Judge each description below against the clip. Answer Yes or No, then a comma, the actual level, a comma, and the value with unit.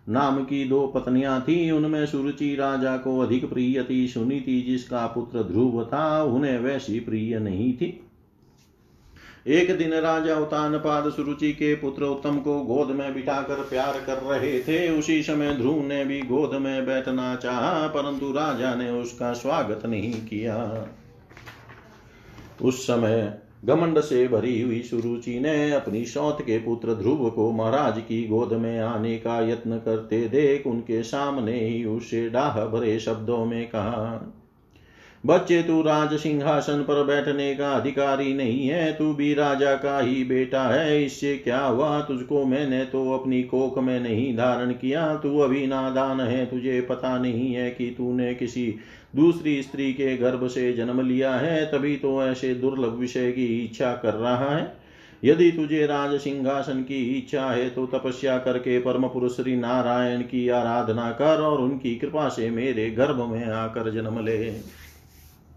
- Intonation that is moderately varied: Yes, average, 3.1 semitones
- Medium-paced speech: Yes, average, 155 wpm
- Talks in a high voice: No, low, 130 Hz